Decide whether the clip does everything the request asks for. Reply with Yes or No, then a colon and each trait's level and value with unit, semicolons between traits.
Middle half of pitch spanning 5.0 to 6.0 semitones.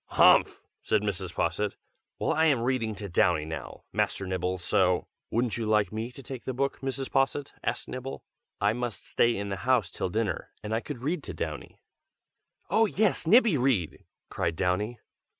Yes: wide, 5.4 semitones